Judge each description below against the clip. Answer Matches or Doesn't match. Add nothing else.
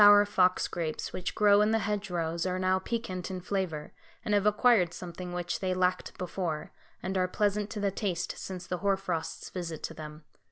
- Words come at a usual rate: Doesn't match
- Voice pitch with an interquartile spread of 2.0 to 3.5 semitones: Matches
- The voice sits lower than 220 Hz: Matches